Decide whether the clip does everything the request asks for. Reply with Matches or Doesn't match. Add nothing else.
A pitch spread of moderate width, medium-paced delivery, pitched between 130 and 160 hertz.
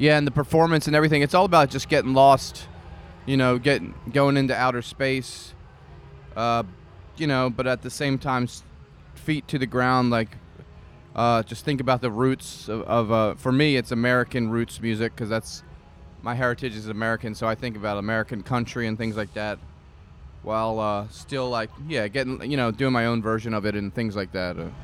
Doesn't match